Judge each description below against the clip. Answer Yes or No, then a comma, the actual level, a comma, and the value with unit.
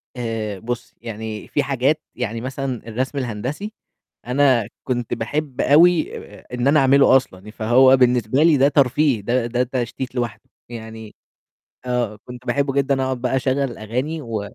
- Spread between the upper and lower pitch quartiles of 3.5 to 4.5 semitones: No, average, 3.1 semitones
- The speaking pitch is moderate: No, low, 125 Hz